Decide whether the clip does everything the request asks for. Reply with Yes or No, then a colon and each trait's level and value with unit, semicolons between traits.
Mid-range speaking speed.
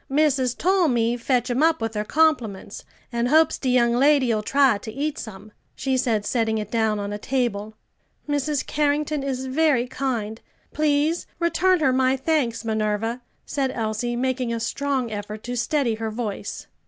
Yes: average, 165 wpm